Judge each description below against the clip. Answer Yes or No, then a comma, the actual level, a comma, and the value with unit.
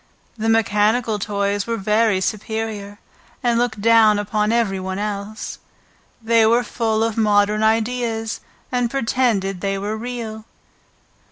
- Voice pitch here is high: Yes, high, 220 Hz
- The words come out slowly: Yes, slow, 125 wpm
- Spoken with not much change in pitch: Yes, narrow, 1.9 semitones